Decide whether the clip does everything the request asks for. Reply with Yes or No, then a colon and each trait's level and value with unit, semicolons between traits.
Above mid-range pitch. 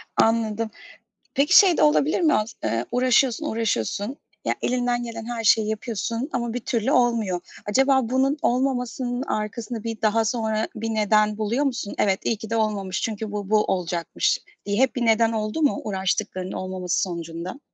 Yes: high, 225 Hz